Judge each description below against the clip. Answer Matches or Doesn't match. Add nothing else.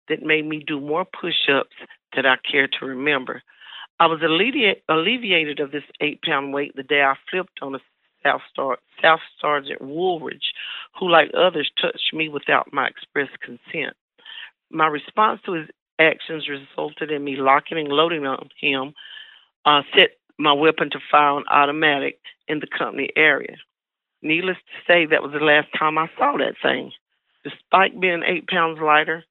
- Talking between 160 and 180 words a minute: Matches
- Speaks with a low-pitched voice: Doesn't match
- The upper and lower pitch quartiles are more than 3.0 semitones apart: Doesn't match